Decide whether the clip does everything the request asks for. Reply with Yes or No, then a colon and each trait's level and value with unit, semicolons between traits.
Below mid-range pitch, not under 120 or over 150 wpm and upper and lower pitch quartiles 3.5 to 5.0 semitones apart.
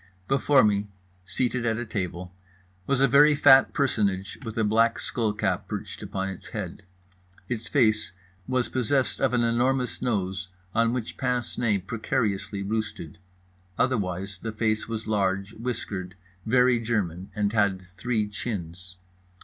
Yes: low, 110 Hz; average, 140 wpm; average, 3.8 semitones